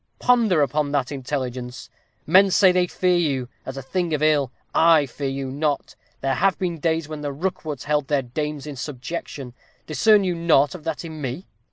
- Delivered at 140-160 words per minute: No, average, 190 wpm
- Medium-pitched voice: Yes, medium, 150 Hz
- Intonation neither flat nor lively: Yes, average, 3.8 semitones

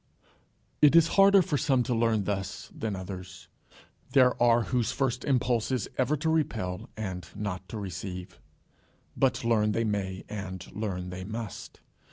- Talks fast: No, average, 160 wpm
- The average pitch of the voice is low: Yes, low, 110 Hz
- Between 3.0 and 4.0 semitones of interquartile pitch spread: No, average, 5.2 semitones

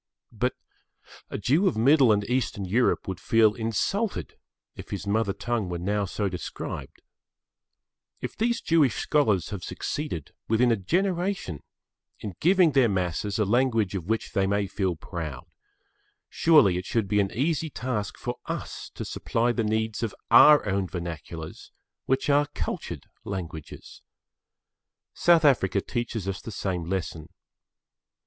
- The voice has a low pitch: Yes, low, 105 Hz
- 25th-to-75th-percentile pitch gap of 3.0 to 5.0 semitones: No, wide, 5.6 semitones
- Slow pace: No, average, 145 wpm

